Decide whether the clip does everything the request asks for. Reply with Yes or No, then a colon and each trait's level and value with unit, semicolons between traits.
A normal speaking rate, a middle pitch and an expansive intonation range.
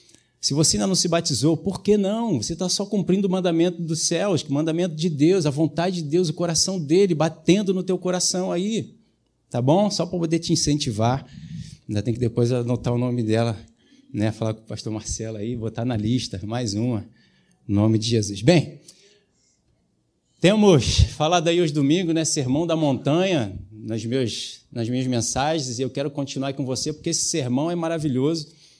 No: fast, 190 wpm; medium, 155 Hz; wide, 6.4 semitones